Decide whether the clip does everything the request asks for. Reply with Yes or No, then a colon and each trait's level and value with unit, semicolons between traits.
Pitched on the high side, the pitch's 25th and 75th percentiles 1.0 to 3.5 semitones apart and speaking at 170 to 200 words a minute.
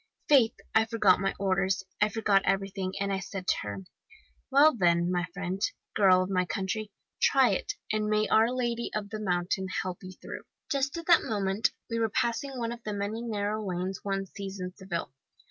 Yes: high, 200 Hz; average, 2.9 semitones; average, 195 wpm